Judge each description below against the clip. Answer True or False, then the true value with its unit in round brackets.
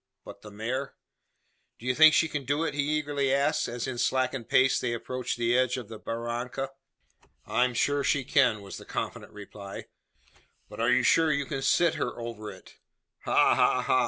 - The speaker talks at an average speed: True (195 wpm)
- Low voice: True (130 Hz)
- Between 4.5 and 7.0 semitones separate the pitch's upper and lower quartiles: False (3.1 semitones)